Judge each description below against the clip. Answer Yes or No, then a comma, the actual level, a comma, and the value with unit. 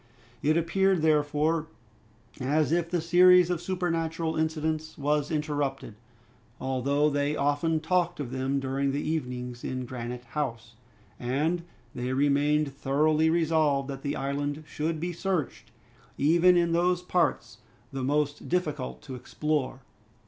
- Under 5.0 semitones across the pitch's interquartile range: Yes, average, 3.1 semitones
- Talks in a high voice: No, medium, 150 Hz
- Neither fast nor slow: No, slow, 130 wpm